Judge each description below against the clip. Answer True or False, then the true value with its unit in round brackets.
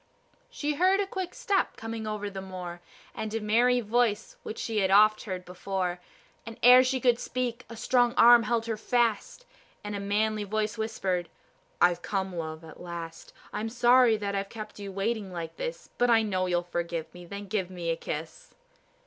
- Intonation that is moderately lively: True (4.3 semitones)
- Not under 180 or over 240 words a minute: True (190 wpm)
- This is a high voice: True (210 Hz)